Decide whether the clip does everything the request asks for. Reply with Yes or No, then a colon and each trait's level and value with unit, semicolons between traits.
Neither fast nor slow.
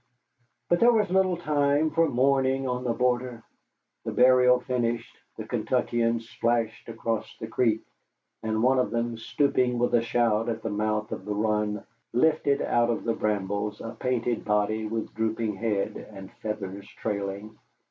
Yes: average, 155 wpm